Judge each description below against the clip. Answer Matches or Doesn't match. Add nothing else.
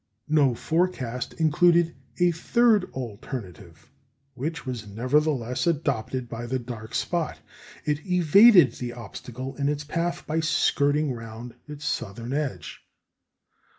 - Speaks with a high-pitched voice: Doesn't match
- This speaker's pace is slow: Matches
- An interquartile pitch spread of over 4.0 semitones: Matches